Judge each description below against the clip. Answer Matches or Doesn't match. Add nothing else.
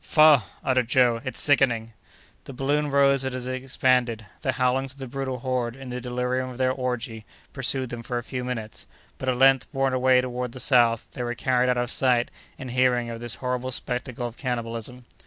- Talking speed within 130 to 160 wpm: Doesn't match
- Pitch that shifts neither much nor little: Doesn't match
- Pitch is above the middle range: Doesn't match